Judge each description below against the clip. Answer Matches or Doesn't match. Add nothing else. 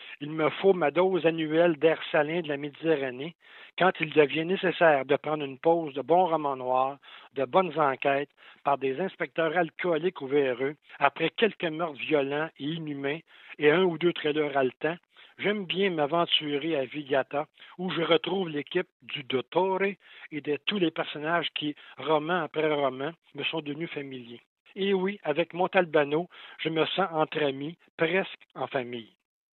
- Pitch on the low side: Doesn't match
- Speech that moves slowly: Doesn't match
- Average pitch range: Matches